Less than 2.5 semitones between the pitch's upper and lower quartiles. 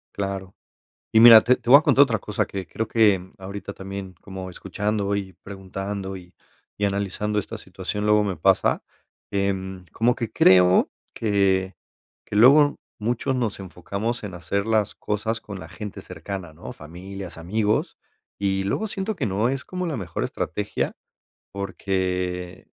No: average, 2.8 semitones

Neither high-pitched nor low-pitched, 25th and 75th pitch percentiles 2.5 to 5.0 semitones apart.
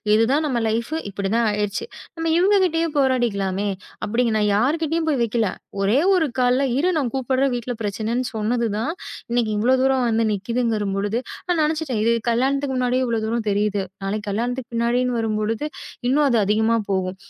No: high, 235 Hz; average, 3.7 semitones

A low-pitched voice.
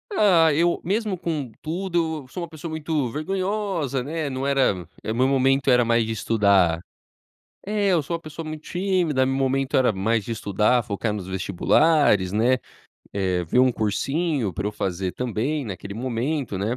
Yes: low, 130 Hz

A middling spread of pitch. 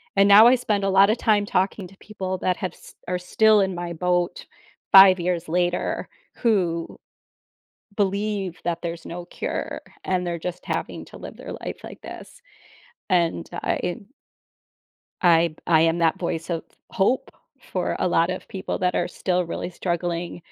No: narrow, 2.3 semitones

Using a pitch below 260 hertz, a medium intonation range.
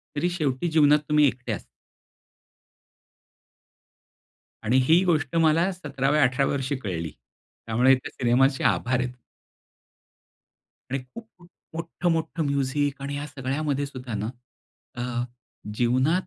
Yes: medium, 140 Hz; average, 3.5 semitones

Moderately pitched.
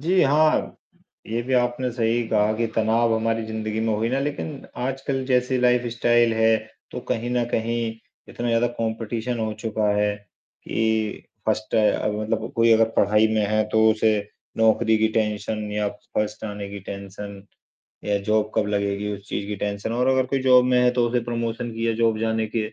No: low, 110 Hz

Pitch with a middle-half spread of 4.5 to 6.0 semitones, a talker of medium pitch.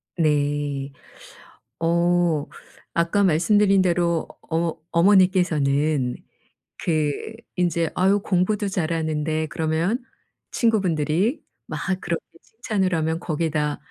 No: average, 3.1 semitones; medium, 170 Hz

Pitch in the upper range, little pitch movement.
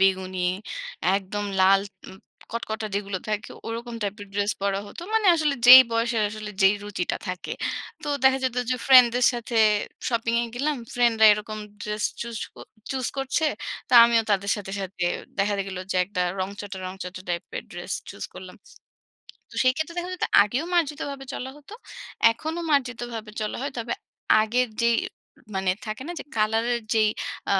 No: high, 225 Hz; average, 3.9 semitones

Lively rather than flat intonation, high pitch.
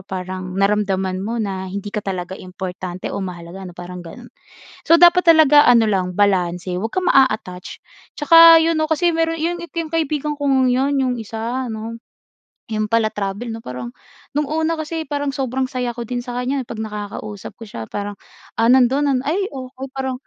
Yes: wide, 6.9 semitones; high, 235 Hz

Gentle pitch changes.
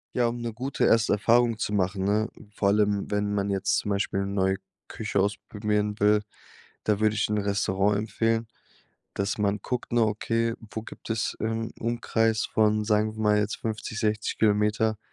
Yes: narrow, 1.5 semitones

